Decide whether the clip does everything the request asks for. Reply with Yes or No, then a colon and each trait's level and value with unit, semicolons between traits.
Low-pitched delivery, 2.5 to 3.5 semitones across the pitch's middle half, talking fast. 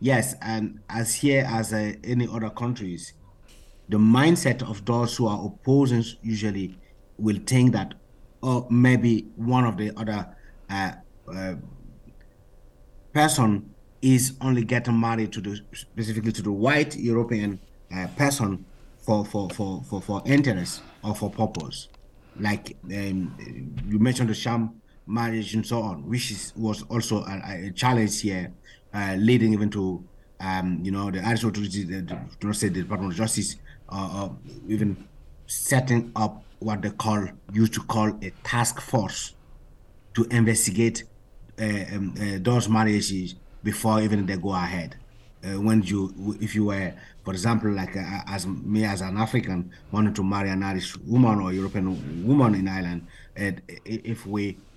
No: low, 105 Hz; average, 2.9 semitones; average, 150 wpm